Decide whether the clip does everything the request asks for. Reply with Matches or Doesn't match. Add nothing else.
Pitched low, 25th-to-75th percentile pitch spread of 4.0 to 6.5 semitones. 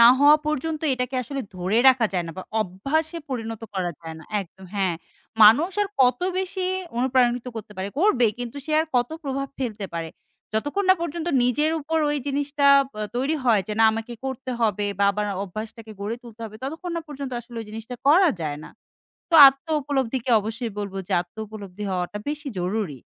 Doesn't match